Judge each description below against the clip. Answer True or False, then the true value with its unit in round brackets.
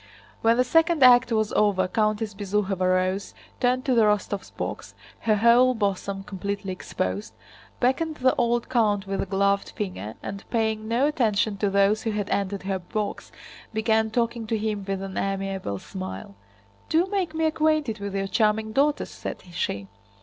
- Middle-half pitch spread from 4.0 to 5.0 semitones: False (3.4 semitones)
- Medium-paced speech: True (160 wpm)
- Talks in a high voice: True (210 Hz)